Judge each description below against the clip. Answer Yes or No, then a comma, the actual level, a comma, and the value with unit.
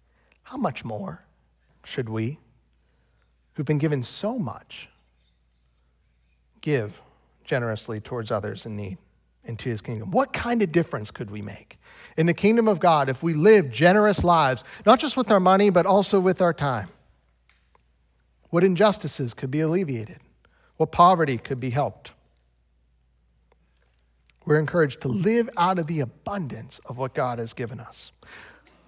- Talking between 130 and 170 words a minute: Yes, average, 145 wpm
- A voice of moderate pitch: No, low, 125 Hz